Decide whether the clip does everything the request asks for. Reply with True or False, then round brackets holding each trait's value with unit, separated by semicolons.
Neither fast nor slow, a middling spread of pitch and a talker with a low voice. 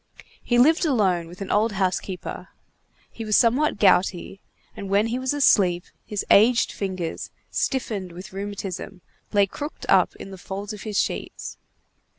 False (155 wpm; 3.5 semitones; 200 Hz)